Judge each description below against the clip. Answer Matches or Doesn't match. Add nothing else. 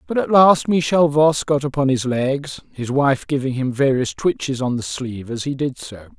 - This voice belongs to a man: Matches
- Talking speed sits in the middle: Doesn't match